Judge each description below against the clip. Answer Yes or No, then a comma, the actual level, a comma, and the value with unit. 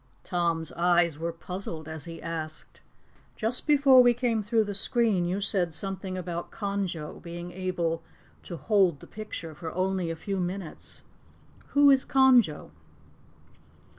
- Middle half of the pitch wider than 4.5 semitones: No, average, 4.0 semitones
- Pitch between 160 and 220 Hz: Yes, medium, 185 Hz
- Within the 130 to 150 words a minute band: Yes, average, 140 wpm